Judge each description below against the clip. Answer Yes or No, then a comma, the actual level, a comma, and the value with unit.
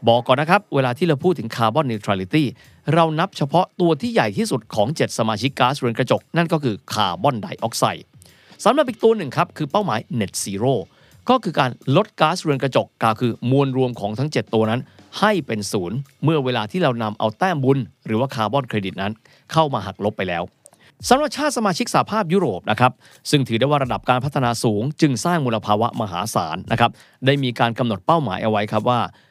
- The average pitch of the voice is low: Yes, low, 130 Hz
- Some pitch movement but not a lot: No, wide, 5.9 semitones